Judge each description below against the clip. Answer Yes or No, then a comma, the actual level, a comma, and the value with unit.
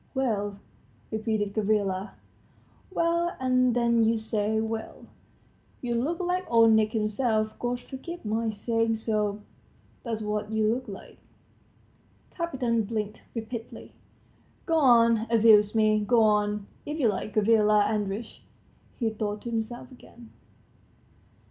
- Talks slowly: Yes, slow, 125 wpm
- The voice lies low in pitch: No, high, 225 Hz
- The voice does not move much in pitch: Yes, narrow, 2.1 semitones